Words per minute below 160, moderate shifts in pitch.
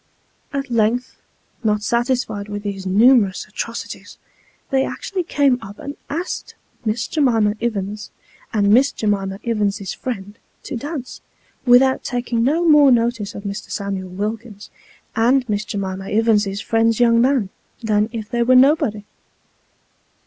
Yes: slow, 135 wpm; average, 3.6 semitones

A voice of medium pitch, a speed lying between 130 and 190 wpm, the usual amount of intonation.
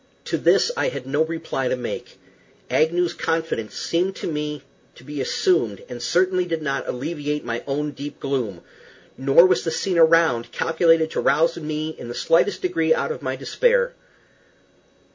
Yes: medium, 155 Hz; average, 165 wpm; average, 3.8 semitones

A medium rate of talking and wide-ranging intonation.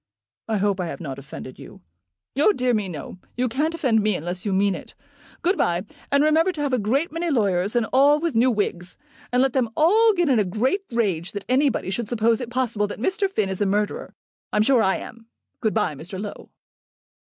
No: fast, 215 wpm; wide, 5.9 semitones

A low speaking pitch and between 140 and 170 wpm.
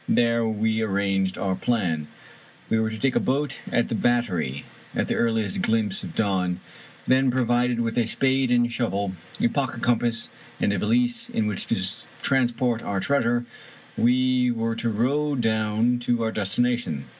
Yes: low, 115 Hz; average, 165 wpm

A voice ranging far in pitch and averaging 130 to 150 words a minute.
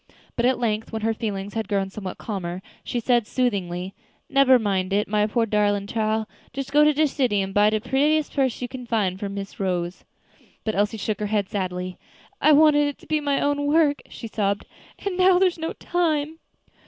No: wide, 6.1 semitones; fast, 205 wpm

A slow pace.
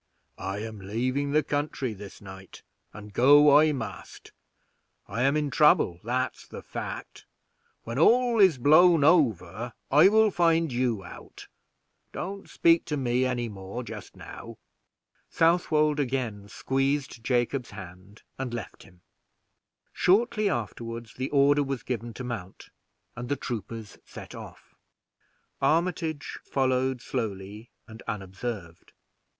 Yes: slow, 125 wpm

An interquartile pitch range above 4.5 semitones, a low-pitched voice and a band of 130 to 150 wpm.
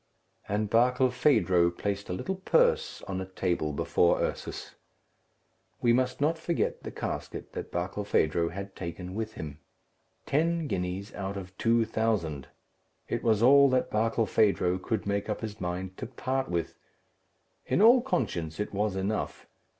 Yes: wide, 5.6 semitones; low, 105 Hz; average, 145 wpm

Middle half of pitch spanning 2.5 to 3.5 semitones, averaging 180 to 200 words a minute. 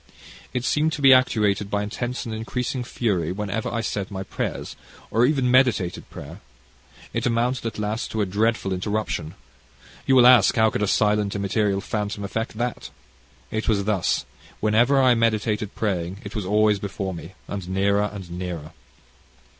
No: average, 2.9 semitones; average, 165 wpm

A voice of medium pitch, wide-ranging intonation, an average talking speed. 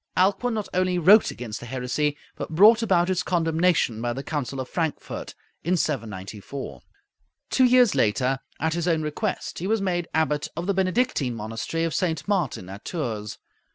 Yes: medium, 160 Hz; wide, 6.4 semitones; average, 170 wpm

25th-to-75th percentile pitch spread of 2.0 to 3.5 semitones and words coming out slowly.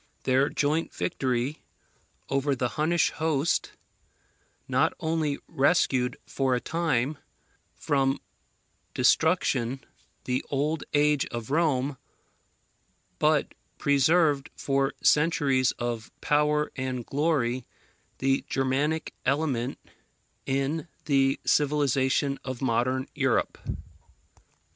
Yes: narrow, 2.5 semitones; slow, 90 wpm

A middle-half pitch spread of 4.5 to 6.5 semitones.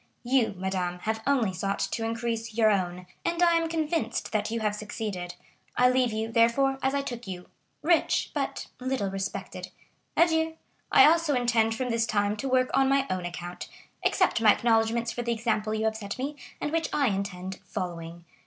Yes: average, 4.8 semitones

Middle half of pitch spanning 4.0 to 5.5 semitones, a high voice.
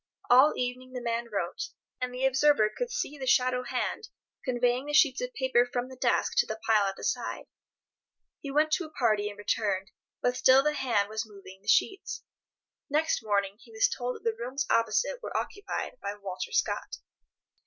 Yes: average, 4.6 semitones; very high, 250 Hz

